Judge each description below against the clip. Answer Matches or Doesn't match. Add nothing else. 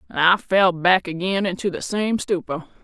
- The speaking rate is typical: Matches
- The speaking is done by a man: Doesn't match